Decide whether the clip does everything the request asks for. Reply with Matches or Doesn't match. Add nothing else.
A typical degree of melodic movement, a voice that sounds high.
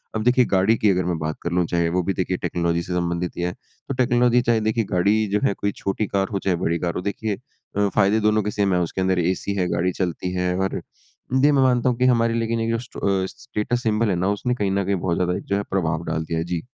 Doesn't match